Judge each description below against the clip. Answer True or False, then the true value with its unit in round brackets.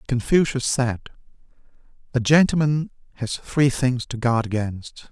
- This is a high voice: False (130 Hz)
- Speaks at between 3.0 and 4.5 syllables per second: True (4.1 syllables/s)